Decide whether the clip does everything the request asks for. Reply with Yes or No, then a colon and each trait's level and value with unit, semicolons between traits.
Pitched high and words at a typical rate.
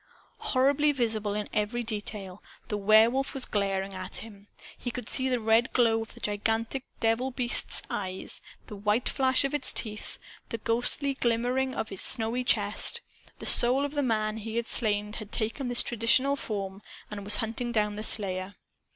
Yes: high, 225 Hz; average, 175 wpm